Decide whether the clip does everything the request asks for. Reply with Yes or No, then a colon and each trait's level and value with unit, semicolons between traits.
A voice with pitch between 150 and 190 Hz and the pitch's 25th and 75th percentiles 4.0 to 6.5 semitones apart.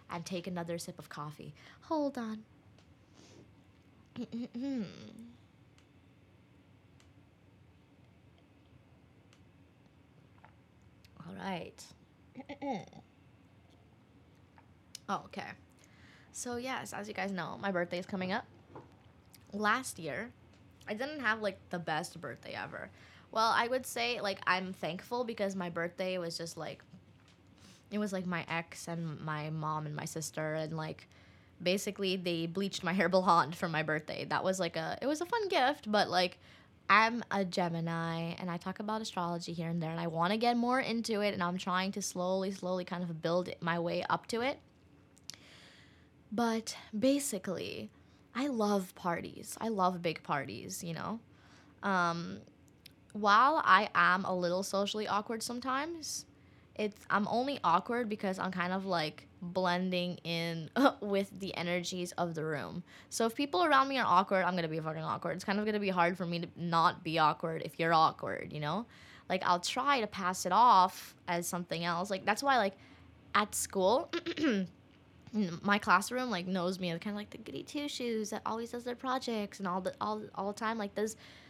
Yes: medium, 185 Hz; average, 4.3 semitones